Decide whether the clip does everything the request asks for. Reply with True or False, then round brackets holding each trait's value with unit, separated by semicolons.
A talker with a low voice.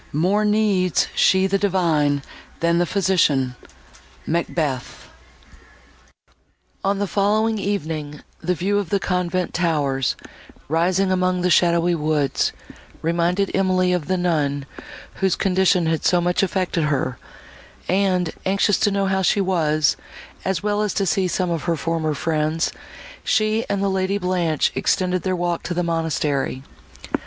False (180 Hz)